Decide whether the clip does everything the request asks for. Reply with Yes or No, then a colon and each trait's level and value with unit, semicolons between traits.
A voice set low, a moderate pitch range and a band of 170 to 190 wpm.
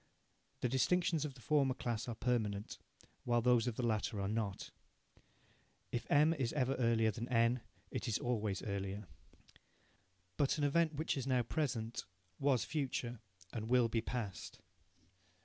No: low, 120 Hz; average, 3.4 semitones; average, 150 wpm